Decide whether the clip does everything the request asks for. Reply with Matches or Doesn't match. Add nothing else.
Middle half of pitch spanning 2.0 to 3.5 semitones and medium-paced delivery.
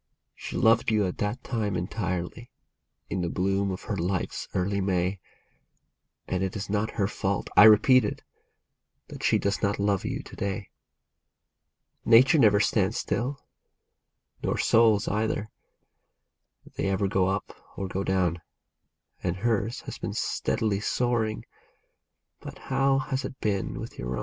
Matches